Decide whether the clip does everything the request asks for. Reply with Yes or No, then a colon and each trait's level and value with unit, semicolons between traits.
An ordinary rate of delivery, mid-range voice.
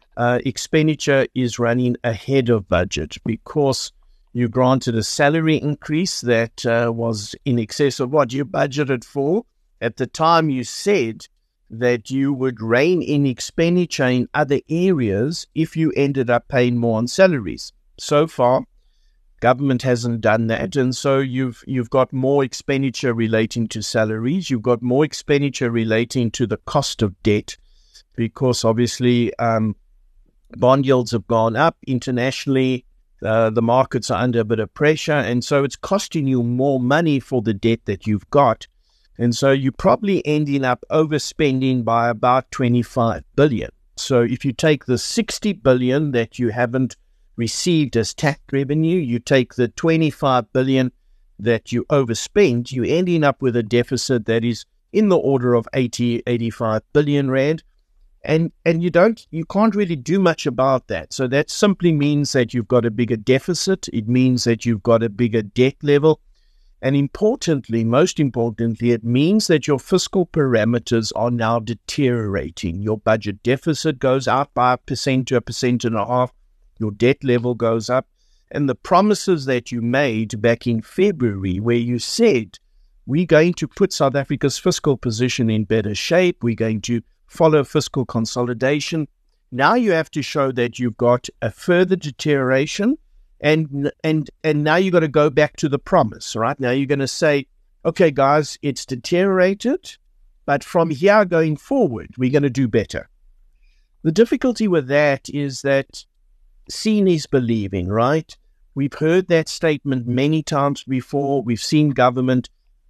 No: average, 160 wpm; low, 130 Hz